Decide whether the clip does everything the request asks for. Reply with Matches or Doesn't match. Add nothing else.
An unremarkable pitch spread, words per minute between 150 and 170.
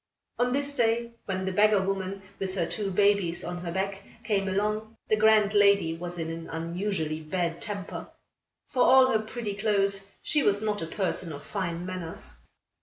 Doesn't match